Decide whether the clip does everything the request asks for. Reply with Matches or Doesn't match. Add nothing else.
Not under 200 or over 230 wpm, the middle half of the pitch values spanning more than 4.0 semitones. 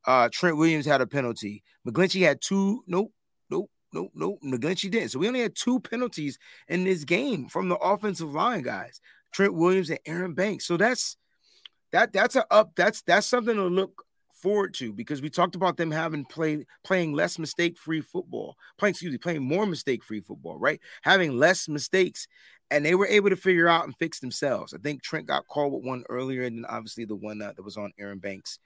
Matches